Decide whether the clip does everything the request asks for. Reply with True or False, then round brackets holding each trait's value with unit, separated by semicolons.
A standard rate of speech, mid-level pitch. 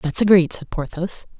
True (170 wpm; 170 Hz)